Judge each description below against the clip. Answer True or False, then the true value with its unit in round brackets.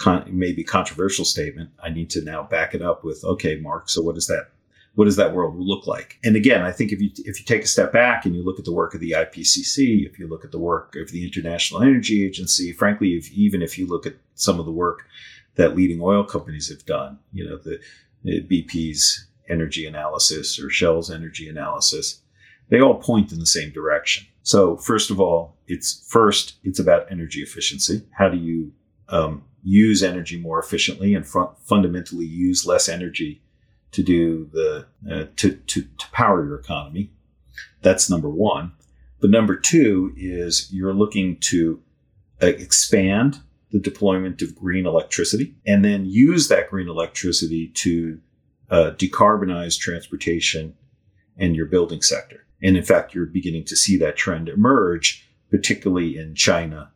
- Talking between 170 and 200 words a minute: True (175 wpm)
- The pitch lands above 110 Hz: False (90 Hz)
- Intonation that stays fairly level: False (3.2 semitones)